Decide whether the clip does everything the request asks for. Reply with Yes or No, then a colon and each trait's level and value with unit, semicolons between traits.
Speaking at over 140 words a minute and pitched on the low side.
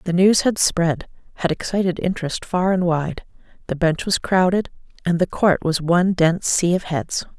No: average, 180 wpm; medium, 175 Hz